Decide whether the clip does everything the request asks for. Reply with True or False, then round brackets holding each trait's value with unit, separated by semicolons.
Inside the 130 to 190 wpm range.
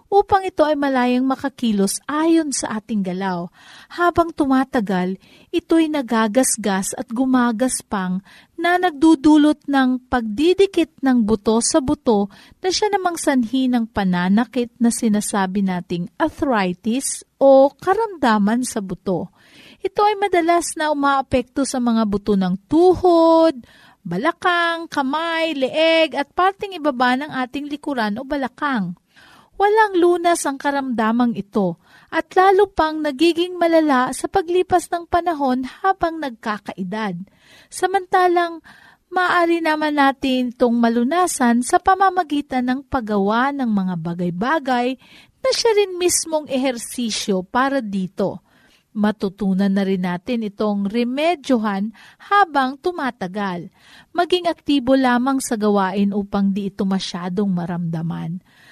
False (115 wpm)